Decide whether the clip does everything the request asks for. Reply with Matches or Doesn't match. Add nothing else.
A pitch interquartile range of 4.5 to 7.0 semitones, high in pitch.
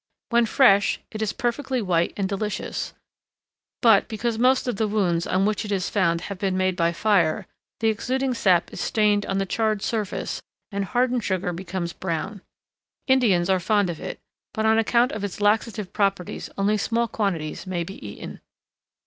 Doesn't match